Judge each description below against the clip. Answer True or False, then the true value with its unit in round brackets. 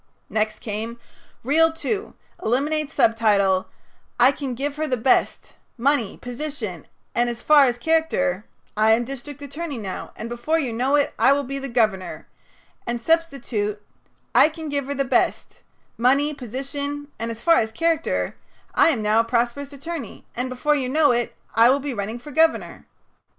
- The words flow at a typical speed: True (170 wpm)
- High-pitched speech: True (260 Hz)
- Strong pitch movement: False (4.0 semitones)